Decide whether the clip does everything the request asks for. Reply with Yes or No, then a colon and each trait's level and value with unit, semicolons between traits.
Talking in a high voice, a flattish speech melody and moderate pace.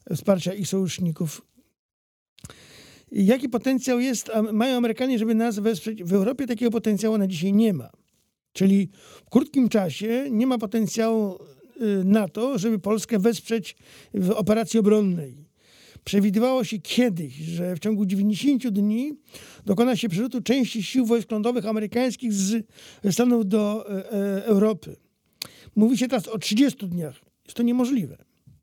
No: high, 220 Hz; average, 3.2 semitones; average, 135 wpm